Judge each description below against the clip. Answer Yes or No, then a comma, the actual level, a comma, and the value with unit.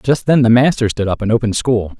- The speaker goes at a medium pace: No, fast, 270 wpm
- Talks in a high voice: No, low, 115 Hz